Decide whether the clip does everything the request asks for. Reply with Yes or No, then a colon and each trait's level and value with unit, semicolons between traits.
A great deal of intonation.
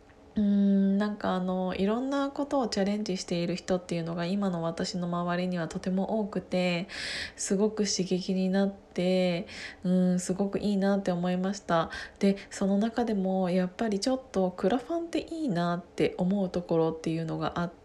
No: narrow, 2.2 semitones